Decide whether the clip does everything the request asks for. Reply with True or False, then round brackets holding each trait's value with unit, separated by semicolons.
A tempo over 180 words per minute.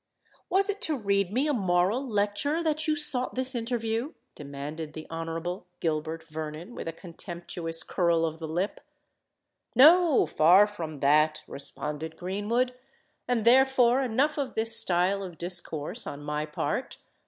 False (140 wpm)